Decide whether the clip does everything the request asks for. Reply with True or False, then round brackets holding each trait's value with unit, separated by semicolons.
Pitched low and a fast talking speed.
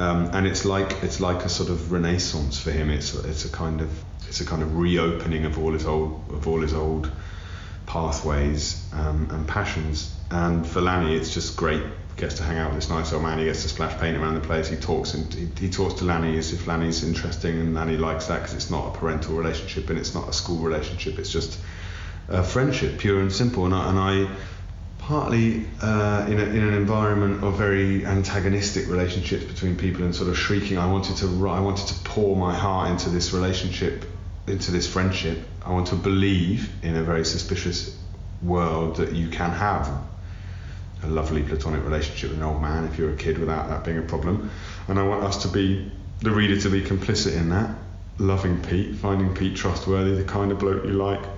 True (90 Hz; 215 wpm)